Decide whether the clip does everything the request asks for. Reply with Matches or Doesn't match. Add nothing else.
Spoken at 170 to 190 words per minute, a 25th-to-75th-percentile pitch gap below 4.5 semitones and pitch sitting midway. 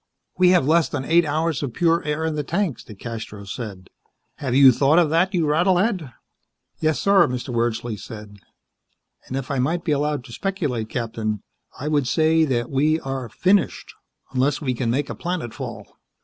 Doesn't match